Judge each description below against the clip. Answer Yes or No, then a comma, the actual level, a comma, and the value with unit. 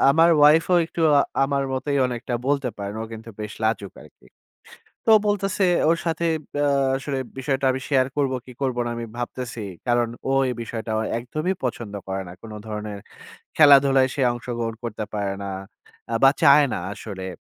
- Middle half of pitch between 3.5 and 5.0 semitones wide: Yes, average, 4.1 semitones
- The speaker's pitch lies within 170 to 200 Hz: No, low, 130 Hz